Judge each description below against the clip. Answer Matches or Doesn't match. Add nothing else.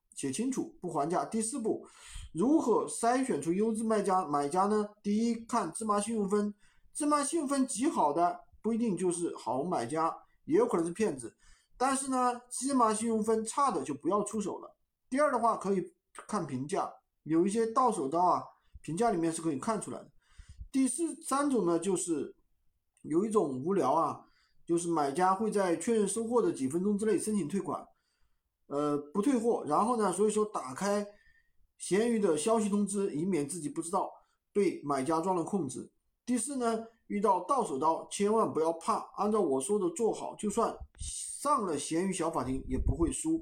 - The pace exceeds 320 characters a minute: Doesn't match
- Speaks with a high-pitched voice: Matches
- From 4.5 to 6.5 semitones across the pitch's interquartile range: Matches